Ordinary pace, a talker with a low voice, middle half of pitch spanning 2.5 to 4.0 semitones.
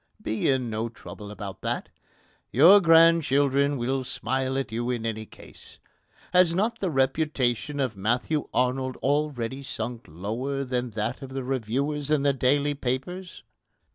Yes: average, 145 wpm; low, 130 Hz; average, 3.4 semitones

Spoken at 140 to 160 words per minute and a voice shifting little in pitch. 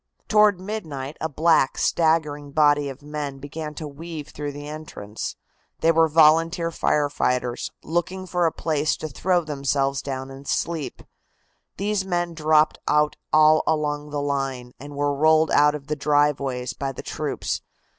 Yes: average, 155 wpm; narrow, 2.3 semitones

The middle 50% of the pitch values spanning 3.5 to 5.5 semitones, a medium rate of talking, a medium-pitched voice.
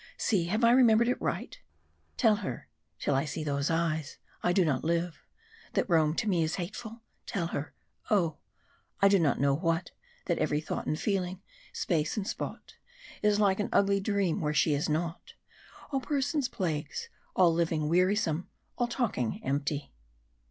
Yes: average, 5.0 semitones; average, 165 wpm; medium, 175 Hz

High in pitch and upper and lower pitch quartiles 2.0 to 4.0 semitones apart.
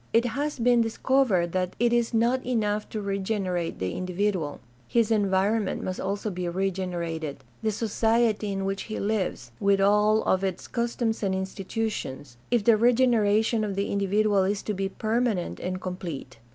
Yes: high, 205 Hz; average, 3.3 semitones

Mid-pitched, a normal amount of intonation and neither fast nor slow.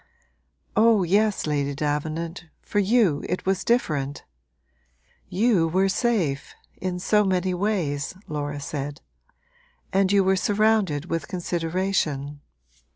No: medium, 180 Hz; average, 5.0 semitones; slow, 110 wpm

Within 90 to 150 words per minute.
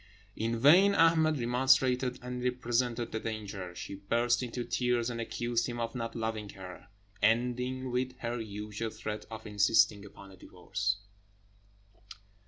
Yes: average, 140 wpm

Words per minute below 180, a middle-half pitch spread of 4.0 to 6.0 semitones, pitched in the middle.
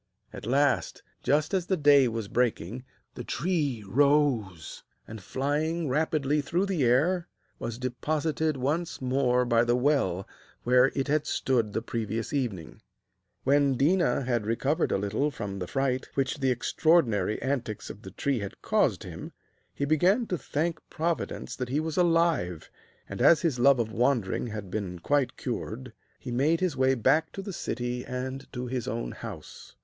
No: average, 165 wpm; average, 4.5 semitones; low, 130 Hz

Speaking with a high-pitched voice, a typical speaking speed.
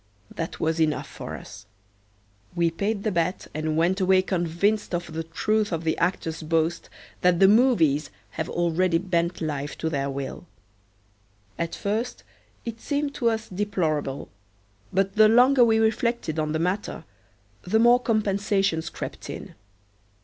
No: medium, 180 Hz; average, 150 wpm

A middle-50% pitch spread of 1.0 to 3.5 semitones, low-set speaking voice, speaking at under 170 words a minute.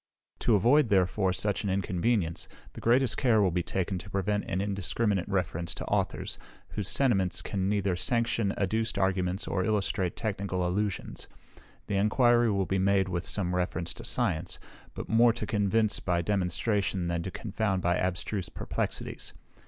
Yes: average, 2.8 semitones; low, 100 Hz; average, 160 wpm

